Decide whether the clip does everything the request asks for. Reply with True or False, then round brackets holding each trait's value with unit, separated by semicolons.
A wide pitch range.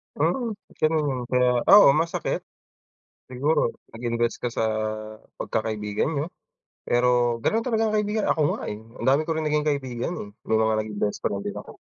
True (6.2 semitones)